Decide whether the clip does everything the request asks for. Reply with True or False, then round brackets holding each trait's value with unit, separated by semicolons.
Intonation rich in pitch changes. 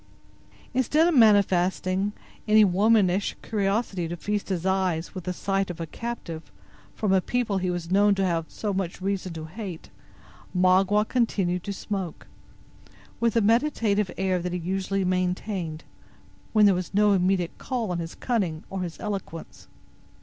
False (2.7 semitones)